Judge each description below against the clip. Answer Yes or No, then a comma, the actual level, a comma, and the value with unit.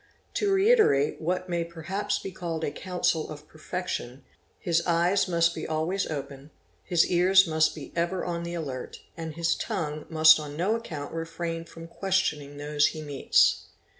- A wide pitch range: No, average, 2.8 semitones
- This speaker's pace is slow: No, average, 165 wpm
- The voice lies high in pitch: No, medium, 165 Hz